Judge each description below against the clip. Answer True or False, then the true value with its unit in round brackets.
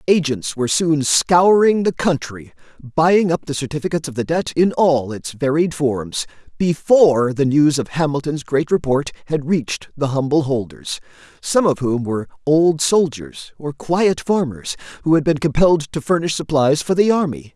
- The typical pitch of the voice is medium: True (150 Hz)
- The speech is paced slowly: False (165 wpm)